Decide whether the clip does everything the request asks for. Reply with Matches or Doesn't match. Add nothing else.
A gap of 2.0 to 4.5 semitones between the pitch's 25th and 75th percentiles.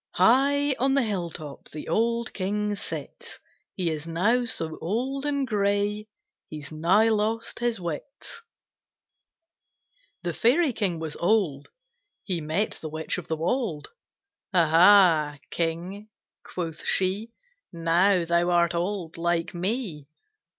Doesn't match